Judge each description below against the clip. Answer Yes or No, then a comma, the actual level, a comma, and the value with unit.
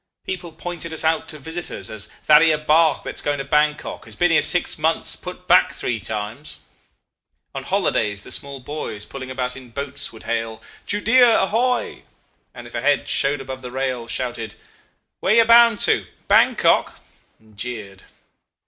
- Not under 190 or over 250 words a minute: No, average, 165 wpm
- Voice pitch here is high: No, medium, 140 Hz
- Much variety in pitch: Yes, wide, 6.2 semitones